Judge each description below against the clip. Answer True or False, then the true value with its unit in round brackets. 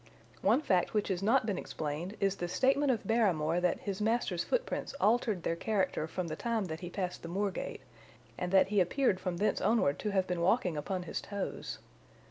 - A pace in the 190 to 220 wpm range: True (205 wpm)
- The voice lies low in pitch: False (190 Hz)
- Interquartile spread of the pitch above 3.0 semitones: True (3.6 semitones)